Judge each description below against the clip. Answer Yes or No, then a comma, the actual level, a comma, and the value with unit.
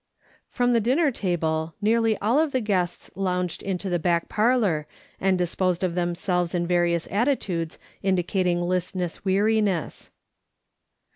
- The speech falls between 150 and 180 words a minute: No, average, 140 wpm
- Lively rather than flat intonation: No, average, 3.5 semitones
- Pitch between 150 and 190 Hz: Yes, medium, 185 Hz